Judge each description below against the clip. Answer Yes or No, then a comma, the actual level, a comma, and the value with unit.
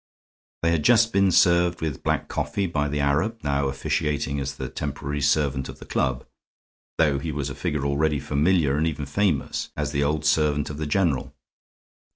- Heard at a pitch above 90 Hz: No, very low, 75 Hz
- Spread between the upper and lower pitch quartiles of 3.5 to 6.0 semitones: No, narrow, 2.6 semitones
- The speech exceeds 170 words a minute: Yes, average, 185 wpm